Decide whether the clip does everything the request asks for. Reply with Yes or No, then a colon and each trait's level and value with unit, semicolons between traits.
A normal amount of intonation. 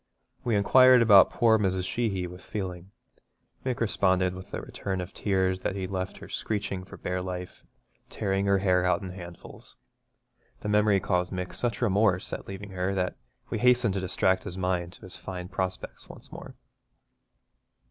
No: narrow, 2.0 semitones